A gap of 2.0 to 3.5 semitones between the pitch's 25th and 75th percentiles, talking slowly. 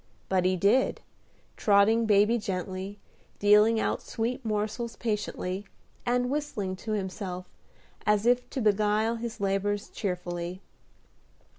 Yes: average, 2.9 semitones; slow, 115 wpm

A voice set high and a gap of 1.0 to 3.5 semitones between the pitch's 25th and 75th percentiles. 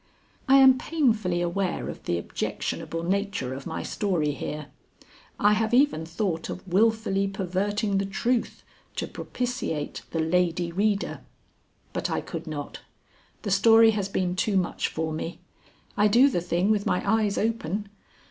No: high, 195 Hz; average, 4.0 semitones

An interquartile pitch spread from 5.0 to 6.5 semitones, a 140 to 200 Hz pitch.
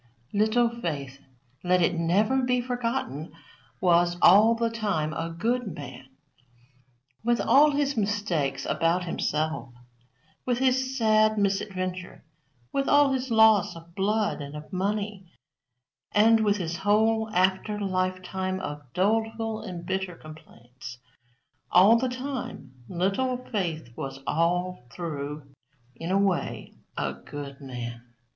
Yes: wide, 5.4 semitones; high, 190 Hz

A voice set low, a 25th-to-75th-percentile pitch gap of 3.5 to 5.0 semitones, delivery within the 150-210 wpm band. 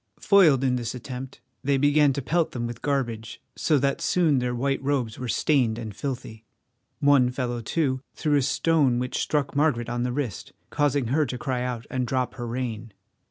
No: low, 130 Hz; average, 2.9 semitones; average, 190 wpm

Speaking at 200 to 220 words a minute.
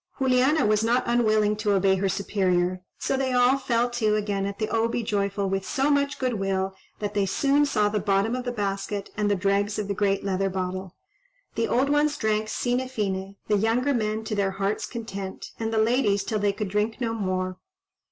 Yes: fast, 205 wpm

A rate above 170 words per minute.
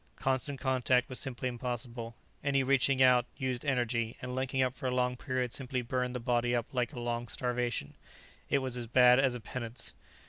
Yes: average, 195 wpm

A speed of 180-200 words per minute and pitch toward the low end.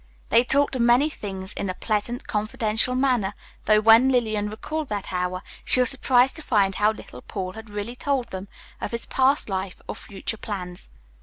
No: average, 185 wpm; high, 220 Hz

